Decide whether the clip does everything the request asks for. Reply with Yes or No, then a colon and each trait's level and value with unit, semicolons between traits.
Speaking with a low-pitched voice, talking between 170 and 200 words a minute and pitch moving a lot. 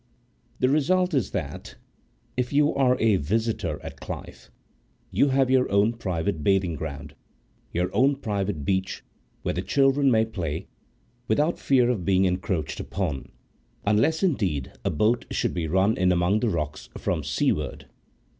No: low, 100 Hz; average, 150 wpm; wide, 7.2 semitones